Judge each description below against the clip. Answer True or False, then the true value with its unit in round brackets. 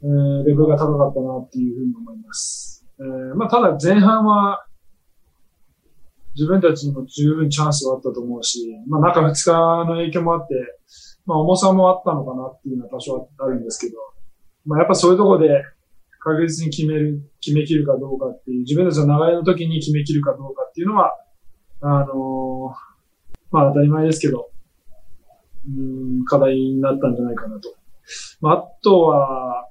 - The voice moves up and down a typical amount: True (4.2 semitones)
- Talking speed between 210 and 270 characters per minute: False (360 characters per minute)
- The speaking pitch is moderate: True (145 Hz)